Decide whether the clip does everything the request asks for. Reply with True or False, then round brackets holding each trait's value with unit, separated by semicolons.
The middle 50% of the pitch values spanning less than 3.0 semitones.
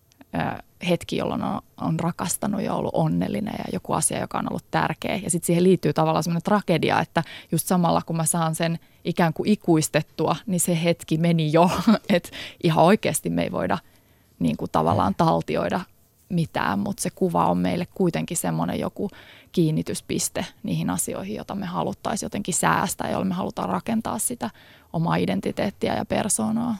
True (2.5 semitones)